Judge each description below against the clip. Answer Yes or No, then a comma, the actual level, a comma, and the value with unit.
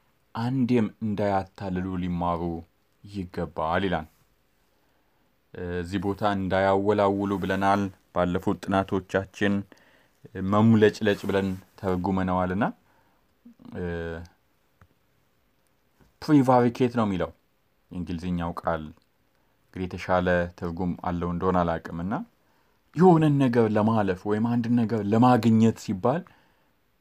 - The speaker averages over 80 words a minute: No, average, 75 wpm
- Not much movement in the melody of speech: No, average, 3.4 semitones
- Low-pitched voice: Yes, very low, 95 Hz